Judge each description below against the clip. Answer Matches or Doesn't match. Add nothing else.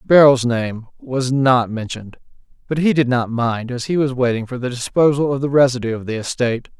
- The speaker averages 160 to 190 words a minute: Doesn't match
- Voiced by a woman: Doesn't match